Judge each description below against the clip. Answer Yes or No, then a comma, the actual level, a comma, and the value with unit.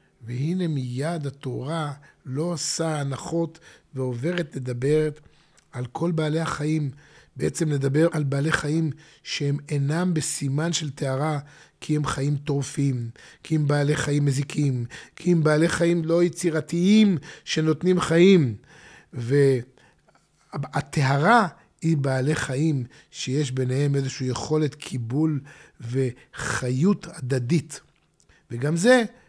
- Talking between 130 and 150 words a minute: No, average, 105 wpm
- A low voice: No, medium, 150 Hz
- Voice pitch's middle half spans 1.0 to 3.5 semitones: Yes, average, 3.0 semitones